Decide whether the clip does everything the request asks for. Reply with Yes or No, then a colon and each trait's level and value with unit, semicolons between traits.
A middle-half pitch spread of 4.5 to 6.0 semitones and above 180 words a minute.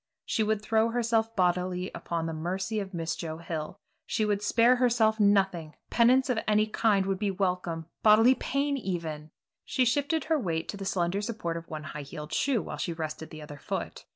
Yes: average, 5.2 semitones; average, 195 wpm